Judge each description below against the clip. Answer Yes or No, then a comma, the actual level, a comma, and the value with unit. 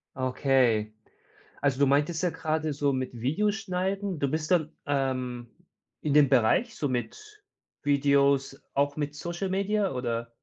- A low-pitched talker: No, medium, 145 Hz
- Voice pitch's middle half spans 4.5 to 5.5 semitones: Yes, average, 4.8 semitones